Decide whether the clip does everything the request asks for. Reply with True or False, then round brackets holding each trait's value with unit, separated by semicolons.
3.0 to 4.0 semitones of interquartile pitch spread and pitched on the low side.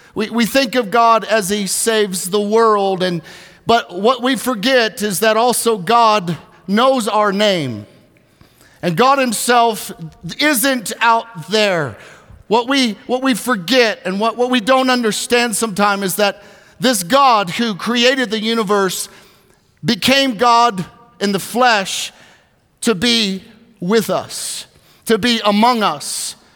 False (3.4 semitones; 225 Hz)